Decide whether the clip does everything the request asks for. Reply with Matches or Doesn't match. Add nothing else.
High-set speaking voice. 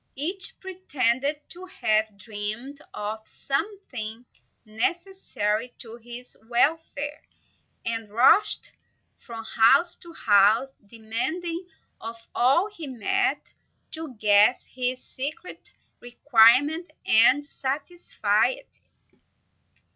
Matches